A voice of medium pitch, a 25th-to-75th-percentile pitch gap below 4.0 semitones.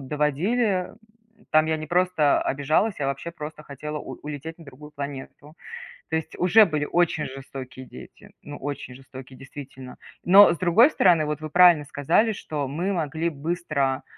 Yes: medium, 150 Hz; average, 3.6 semitones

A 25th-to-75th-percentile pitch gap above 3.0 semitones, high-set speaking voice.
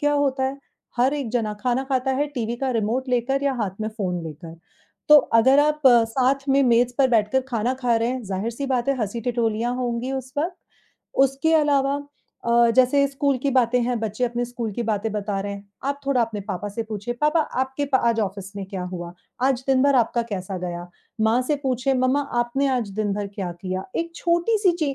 Yes: average, 4.0 semitones; high, 245 Hz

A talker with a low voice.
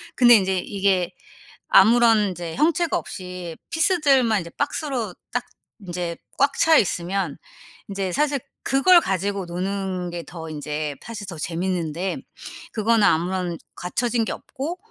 No: high, 195 Hz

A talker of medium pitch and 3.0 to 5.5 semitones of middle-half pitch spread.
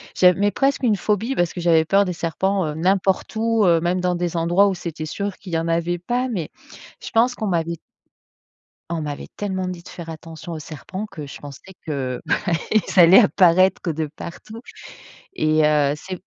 Yes: medium, 175 Hz; average, 3.4 semitones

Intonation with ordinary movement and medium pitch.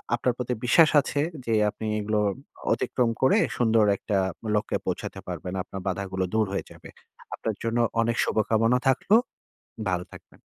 No: average, 3.5 semitones; low, 110 Hz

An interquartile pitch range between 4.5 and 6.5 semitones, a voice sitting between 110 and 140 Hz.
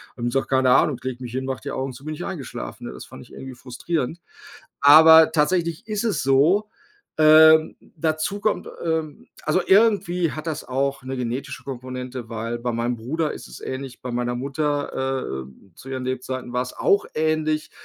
No: average, 3.9 semitones; low, 135 Hz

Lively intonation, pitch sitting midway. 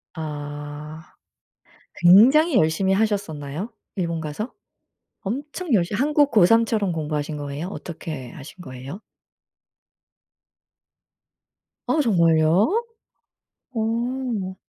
Yes: wide, 6.8 semitones; medium, 180 Hz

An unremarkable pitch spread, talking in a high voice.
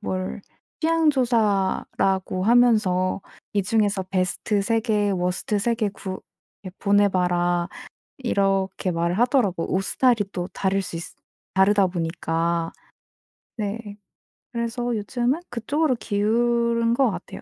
Yes: average, 3.9 semitones; high, 205 Hz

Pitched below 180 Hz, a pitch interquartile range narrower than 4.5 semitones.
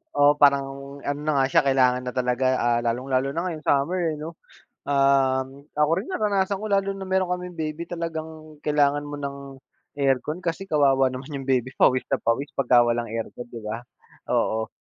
Yes: medium, 140 Hz; average, 3.6 semitones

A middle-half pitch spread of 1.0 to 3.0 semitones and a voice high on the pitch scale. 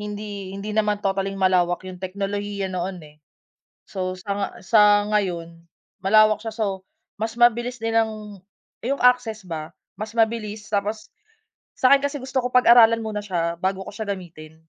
Yes: average, 2.7 semitones; high, 205 Hz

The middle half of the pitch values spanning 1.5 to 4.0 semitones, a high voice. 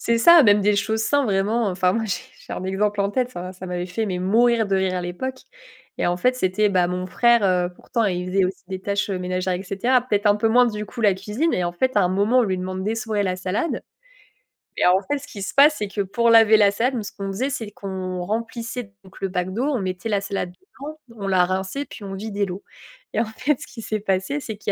Yes: average, 3.7 semitones; high, 205 Hz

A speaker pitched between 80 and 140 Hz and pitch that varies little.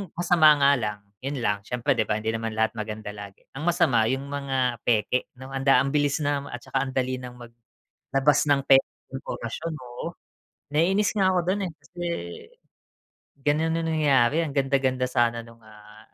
No: low, 135 Hz; average, 3.9 semitones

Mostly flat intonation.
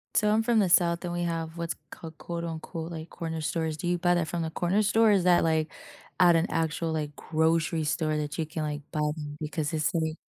Yes: narrow, 1.7 semitones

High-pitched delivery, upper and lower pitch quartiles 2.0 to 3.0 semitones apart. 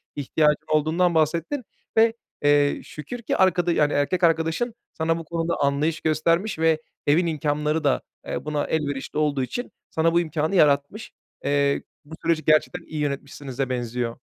No: medium, 155 Hz; narrow, 2.5 semitones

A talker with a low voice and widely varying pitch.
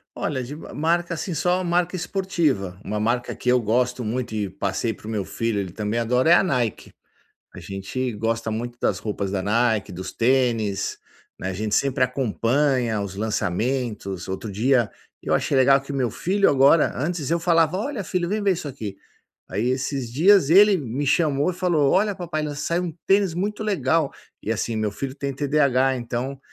Yes: low, 130 Hz; wide, 6.8 semitones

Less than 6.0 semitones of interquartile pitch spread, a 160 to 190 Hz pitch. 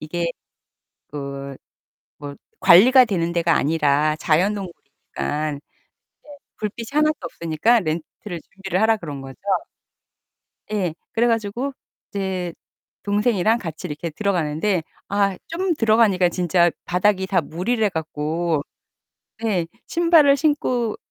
Yes: wide, 5.5 semitones; medium, 185 Hz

